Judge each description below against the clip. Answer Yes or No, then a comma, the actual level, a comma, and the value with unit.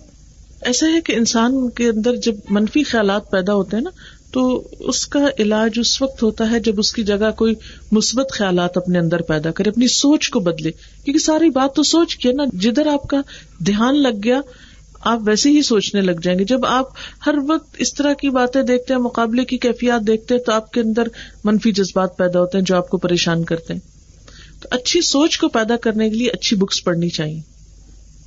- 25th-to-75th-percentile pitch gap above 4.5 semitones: Yes, average, 5.1 semitones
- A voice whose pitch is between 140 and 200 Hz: No, high, 230 Hz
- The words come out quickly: Yes, fast, 210 wpm